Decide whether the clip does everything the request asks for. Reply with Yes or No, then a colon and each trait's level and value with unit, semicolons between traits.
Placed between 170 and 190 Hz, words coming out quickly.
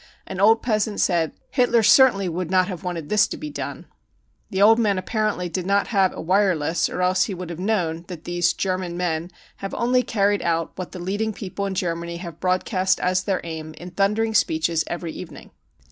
Yes: medium, 185 Hz; fast, 215 wpm